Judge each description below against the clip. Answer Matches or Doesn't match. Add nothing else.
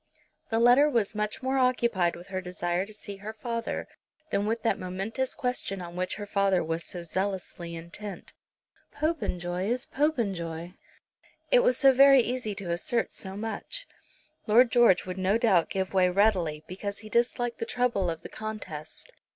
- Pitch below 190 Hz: Doesn't match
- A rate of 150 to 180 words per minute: Matches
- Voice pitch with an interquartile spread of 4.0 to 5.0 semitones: Matches